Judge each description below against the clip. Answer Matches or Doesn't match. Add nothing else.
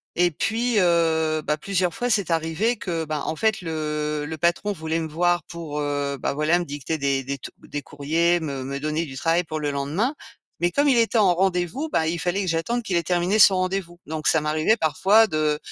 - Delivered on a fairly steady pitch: Doesn't match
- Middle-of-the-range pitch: Matches